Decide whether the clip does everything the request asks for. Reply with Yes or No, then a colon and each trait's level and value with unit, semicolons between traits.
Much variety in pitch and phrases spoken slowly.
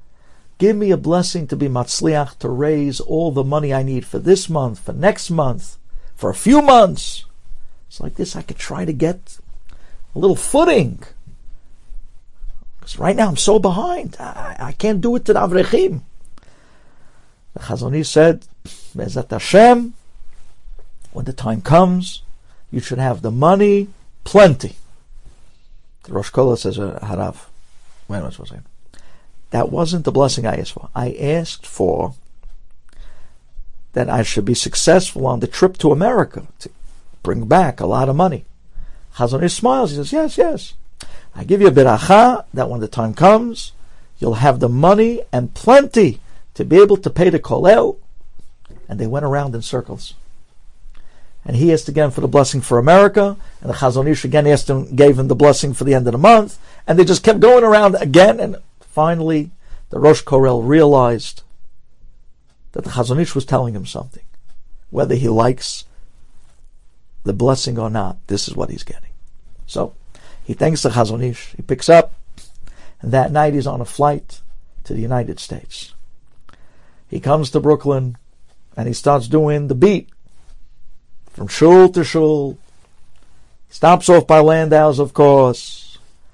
No: wide, 6.3 semitones; average, 160 wpm